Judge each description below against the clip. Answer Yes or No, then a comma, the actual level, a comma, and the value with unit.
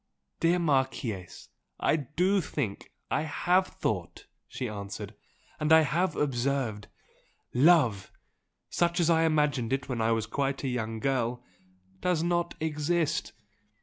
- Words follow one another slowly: Yes, slow, 130 wpm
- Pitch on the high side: No, medium, 140 Hz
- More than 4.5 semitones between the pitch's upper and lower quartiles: Yes, wide, 5.6 semitones